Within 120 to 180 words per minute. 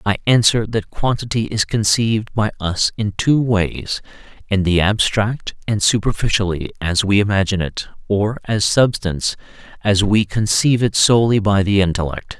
Yes: average, 150 wpm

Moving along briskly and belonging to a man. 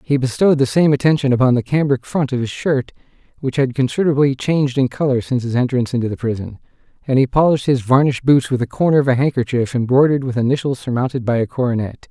Yes: fast, 215 wpm; male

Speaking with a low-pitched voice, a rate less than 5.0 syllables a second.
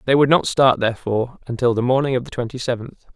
No: low, 125 Hz; 6.6 syllables/s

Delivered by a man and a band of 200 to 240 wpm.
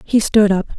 No: female; fast, 230 wpm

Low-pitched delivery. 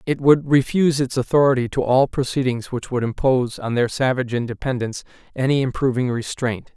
Yes: low, 130 Hz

